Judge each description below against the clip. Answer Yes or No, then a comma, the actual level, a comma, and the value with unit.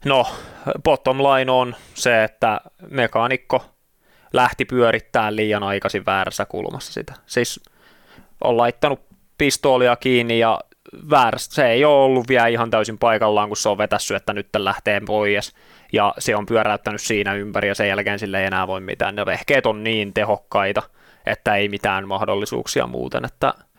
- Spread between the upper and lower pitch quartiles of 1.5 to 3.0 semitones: Yes, narrow, 2.6 semitones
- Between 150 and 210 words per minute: Yes, fast, 155 wpm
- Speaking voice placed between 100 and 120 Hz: Yes, low, 105 Hz